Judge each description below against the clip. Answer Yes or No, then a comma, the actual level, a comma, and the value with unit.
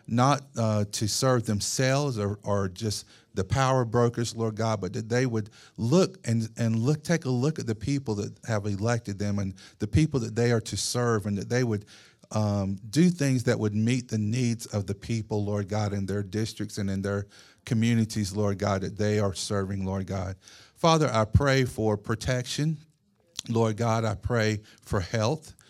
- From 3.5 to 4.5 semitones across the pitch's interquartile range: No, average, 3.0 semitones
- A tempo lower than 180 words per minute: No, average, 190 wpm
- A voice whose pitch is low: Yes, low, 110 Hz